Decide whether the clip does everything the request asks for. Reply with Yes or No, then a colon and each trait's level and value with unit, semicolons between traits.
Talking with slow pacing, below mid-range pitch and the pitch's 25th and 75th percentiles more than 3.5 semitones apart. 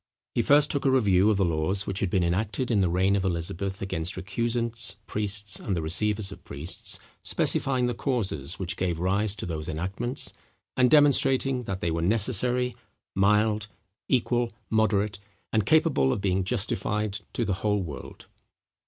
No: average, 165 wpm; low, 100 Hz; average, 4.2 semitones